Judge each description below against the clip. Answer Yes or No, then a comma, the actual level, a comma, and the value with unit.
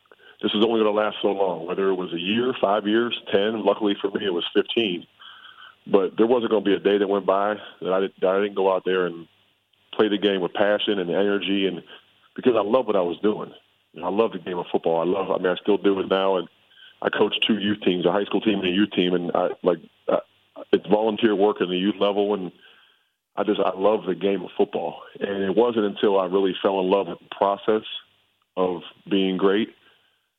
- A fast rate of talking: Yes, fast, 235 wpm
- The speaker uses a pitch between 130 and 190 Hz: No, low, 100 Hz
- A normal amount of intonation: No, narrow, 1.9 semitones